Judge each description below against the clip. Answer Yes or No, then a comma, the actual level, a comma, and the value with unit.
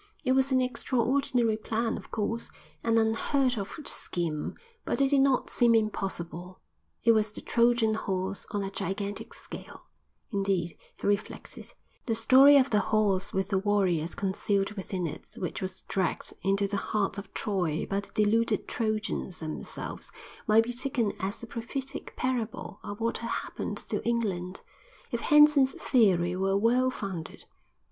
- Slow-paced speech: No, average, 155 wpm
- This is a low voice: No, high, 215 Hz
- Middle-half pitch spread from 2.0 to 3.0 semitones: No, average, 3.5 semitones